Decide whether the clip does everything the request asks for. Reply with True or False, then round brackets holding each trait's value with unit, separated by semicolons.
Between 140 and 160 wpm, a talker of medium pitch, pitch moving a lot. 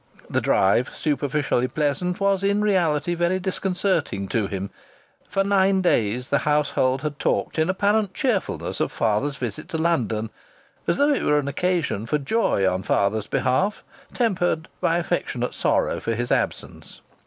True (155 wpm; 155 Hz; 7.1 semitones)